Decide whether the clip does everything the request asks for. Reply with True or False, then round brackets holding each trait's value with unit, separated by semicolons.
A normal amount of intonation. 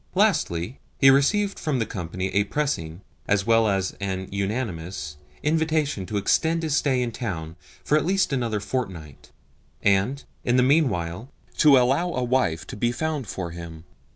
False (7.3 semitones)